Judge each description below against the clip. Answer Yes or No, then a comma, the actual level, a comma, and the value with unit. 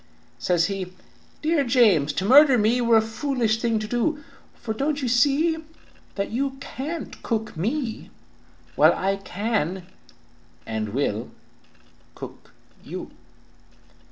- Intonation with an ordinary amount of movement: No, wide, 5.7 semitones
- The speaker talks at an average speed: No, slow, 125 wpm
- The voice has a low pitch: No, high, 230 Hz